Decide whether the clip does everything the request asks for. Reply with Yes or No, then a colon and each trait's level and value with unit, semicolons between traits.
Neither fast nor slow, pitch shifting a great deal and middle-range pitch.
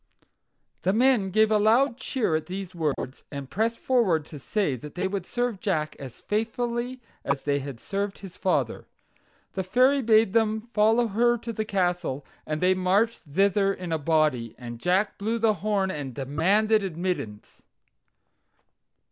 No: average, 160 wpm; wide, 5.9 semitones; high, 195 Hz